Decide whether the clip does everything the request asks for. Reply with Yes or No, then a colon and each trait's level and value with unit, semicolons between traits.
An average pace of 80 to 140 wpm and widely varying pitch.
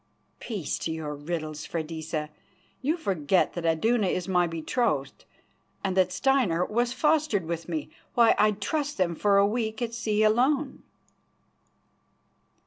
Yes: slow, 135 wpm; wide, 6.3 semitones